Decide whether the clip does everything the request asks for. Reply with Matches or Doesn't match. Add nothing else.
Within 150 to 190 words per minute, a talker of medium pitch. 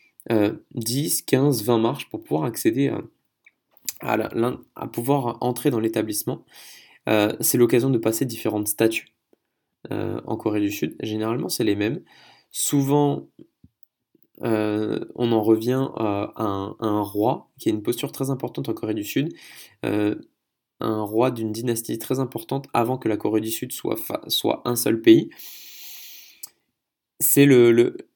Doesn't match